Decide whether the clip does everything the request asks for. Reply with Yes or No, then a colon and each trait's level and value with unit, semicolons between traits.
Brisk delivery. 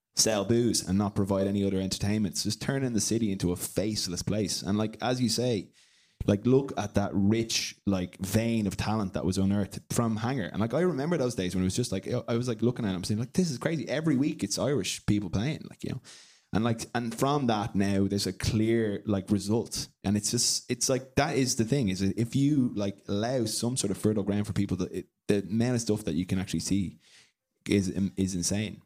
Yes: fast, 230 wpm